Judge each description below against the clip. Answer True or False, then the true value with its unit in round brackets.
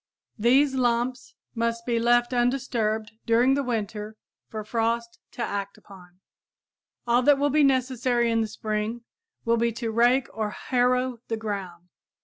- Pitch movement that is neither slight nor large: False (2.3 semitones)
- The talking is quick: False (145 wpm)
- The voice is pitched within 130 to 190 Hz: False (235 Hz)